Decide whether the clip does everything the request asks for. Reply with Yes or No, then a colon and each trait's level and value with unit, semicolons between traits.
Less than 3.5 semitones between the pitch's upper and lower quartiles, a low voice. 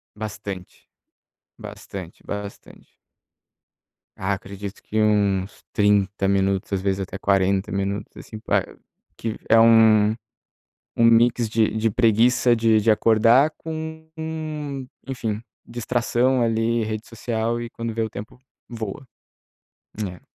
Yes: average, 2.7 semitones; low, 110 Hz